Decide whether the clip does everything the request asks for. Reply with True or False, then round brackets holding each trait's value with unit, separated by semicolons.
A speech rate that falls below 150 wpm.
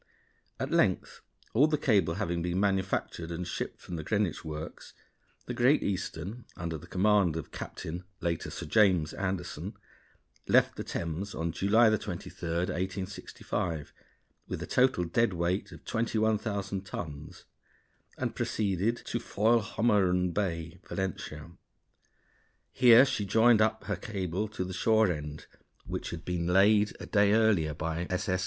True (140 wpm)